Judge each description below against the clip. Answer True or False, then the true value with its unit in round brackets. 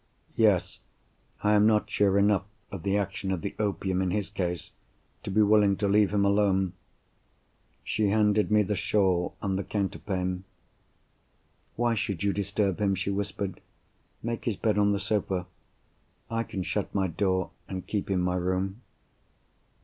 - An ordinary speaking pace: True (160 wpm)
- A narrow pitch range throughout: True (1.8 semitones)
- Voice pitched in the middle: False (100 Hz)